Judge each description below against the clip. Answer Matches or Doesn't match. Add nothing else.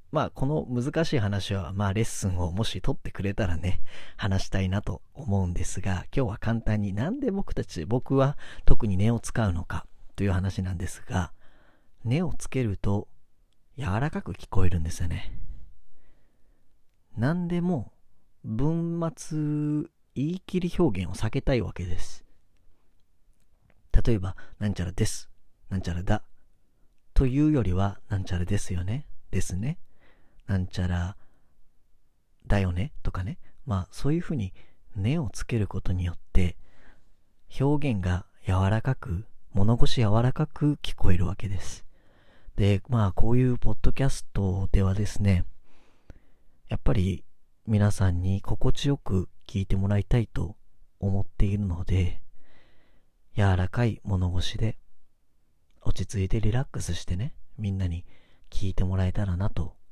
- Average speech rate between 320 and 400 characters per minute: Doesn't match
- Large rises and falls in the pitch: Doesn't match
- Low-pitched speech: Matches